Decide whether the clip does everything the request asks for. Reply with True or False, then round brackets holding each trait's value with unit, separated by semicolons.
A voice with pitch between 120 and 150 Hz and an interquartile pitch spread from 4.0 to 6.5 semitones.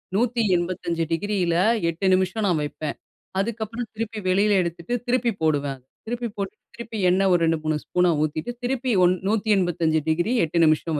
False (185 Hz; 5.1 semitones)